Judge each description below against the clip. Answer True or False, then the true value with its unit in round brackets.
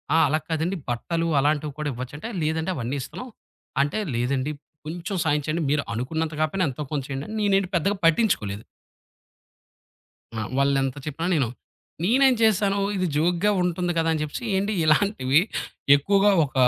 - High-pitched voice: False (160 Hz)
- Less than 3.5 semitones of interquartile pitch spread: False (5.2 semitones)